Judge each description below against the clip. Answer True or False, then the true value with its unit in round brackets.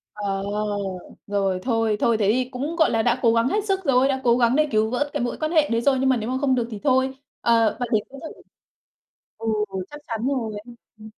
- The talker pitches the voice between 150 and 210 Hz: False (245 Hz)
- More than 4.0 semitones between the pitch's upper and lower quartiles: False (3.1 semitones)